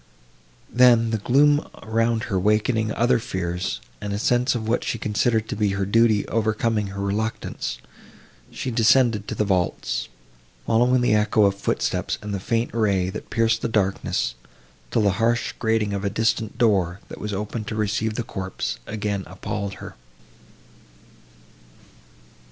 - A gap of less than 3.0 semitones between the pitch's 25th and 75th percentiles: Yes, narrow, 2.4 semitones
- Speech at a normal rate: Yes, average, 155 wpm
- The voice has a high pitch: No, low, 110 Hz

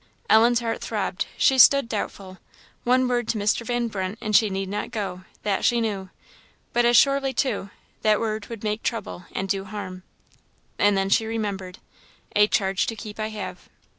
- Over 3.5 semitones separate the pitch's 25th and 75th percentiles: No, average, 3.1 semitones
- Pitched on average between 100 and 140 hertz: No, high, 215 Hz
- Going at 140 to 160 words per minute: No, average, 180 wpm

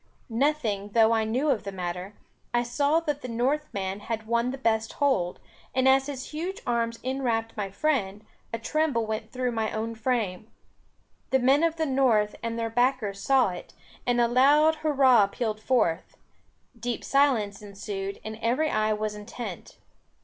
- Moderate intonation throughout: Yes, average, 3.8 semitones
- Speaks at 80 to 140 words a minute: No, average, 170 wpm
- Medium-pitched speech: No, high, 230 Hz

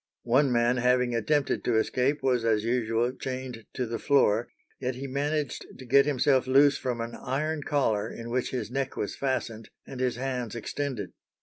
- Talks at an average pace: Yes, average, 180 wpm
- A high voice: No, low, 125 Hz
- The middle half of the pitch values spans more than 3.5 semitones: No, narrow, 2.6 semitones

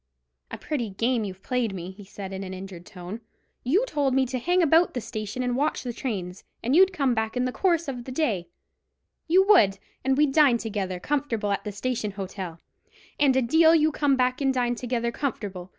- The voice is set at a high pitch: Yes, high, 245 Hz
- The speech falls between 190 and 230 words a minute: Yes, average, 200 wpm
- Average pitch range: No, wide, 6.0 semitones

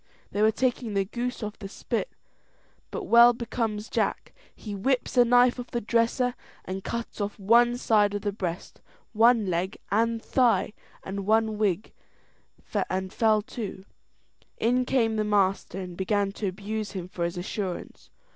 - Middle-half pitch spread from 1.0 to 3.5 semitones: Yes, average, 3.2 semitones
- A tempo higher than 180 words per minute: No, average, 160 wpm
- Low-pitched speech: No, high, 215 Hz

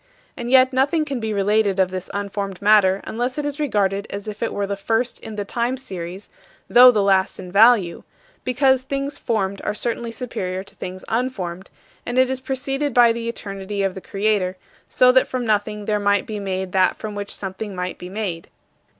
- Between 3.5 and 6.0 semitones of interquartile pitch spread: Yes, average, 4.2 semitones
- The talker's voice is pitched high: Yes, high, 210 Hz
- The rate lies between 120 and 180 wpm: No, average, 200 wpm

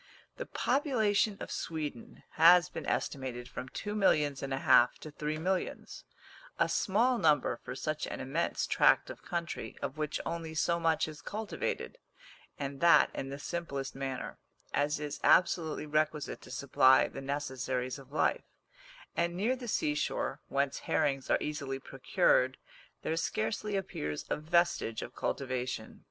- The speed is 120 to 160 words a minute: Yes, average, 150 wpm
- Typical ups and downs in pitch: Yes, average, 4.2 semitones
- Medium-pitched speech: Yes, medium, 150 Hz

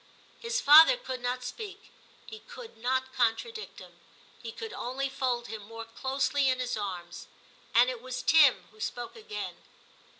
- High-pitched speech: Yes, very high, 255 Hz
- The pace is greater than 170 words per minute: No, average, 165 wpm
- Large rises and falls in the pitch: Yes, wide, 8.0 semitones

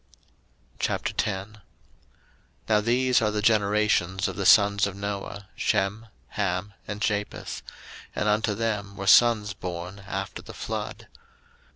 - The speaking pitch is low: Yes, low, 105 Hz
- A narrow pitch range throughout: Yes, narrow, 1.5 semitones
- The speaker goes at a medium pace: No, slow, 125 wpm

